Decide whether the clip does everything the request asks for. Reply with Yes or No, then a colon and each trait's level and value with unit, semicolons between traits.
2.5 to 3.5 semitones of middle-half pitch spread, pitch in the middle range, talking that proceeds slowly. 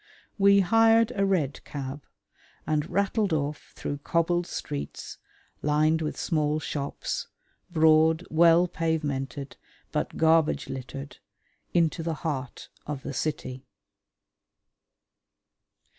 Yes: average, 3.0 semitones; medium, 155 Hz; slow, 100 wpm